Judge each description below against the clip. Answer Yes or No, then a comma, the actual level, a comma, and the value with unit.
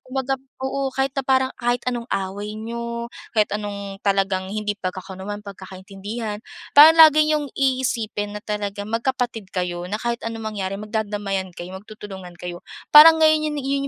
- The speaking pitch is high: Yes, high, 215 Hz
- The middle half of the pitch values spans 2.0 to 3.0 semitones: No, average, 4.9 semitones